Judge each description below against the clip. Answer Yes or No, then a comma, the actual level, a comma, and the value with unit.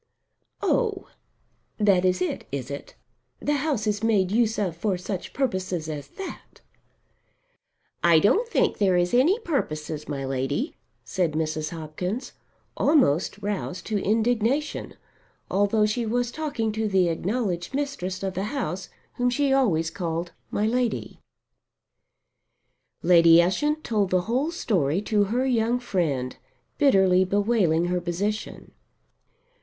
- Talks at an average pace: No, slow, 130 wpm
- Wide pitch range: Yes, wide, 5.8 semitones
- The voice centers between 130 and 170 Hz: No, high, 200 Hz